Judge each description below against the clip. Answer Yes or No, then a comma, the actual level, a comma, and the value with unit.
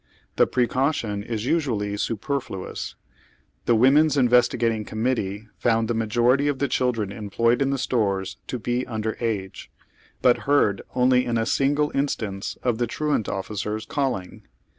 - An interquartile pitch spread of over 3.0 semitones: Yes, average, 3.4 semitones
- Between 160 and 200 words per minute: No, average, 150 wpm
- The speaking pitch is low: Yes, low, 120 Hz